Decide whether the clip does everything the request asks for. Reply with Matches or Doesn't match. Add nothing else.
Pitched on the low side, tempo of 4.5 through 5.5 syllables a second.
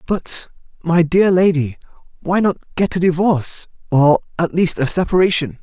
Doesn't match